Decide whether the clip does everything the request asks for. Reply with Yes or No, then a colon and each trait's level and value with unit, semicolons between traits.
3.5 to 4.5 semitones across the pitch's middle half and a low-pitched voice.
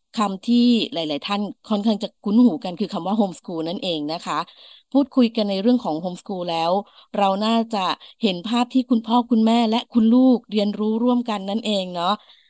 No: average, 4.0 semitones; high, 210 Hz